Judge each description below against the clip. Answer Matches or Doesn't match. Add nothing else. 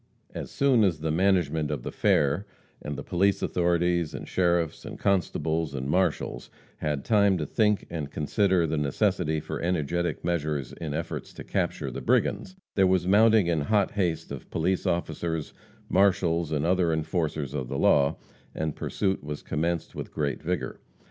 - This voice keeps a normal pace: Matches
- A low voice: Matches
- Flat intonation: Doesn't match